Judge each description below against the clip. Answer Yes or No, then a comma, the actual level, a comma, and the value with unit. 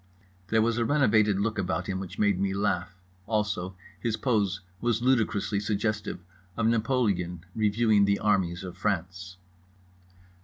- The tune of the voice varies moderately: Yes, average, 3.0 semitones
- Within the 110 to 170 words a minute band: Yes, average, 140 wpm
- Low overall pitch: Yes, low, 105 Hz